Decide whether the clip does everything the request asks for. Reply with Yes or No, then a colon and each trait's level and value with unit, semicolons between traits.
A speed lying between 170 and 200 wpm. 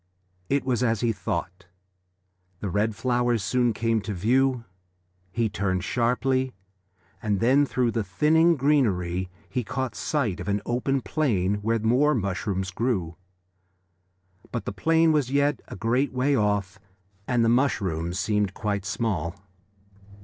No: average, 140 wpm